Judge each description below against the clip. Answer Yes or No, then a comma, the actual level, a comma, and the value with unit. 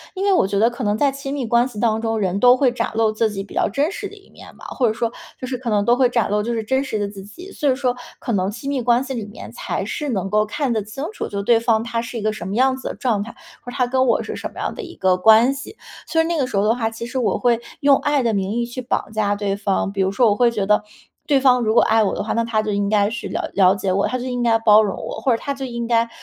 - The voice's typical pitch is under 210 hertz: No, high, 230 Hz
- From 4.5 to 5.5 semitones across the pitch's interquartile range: No, average, 3.6 semitones